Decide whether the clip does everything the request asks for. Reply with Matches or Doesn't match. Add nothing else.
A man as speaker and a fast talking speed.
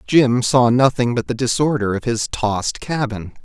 Doesn't match